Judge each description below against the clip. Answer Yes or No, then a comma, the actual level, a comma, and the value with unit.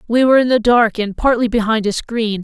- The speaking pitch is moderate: No, high, 230 Hz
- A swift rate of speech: Yes, fast, 245 wpm